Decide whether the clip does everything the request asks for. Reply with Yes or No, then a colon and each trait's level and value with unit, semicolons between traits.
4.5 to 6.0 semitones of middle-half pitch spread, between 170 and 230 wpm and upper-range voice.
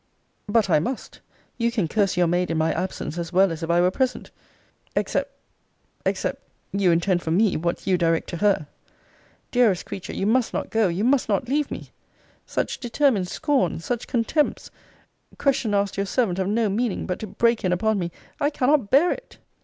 Yes: average, 5.3 semitones; average, 190 wpm; high, 200 Hz